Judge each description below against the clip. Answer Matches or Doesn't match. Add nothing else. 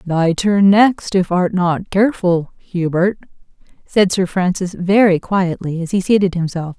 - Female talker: Matches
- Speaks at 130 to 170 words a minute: Matches